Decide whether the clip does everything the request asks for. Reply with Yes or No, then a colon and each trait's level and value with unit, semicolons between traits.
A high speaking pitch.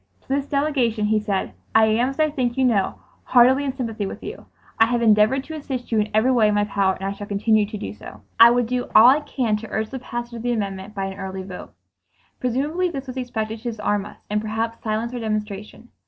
Yes: high, 225 Hz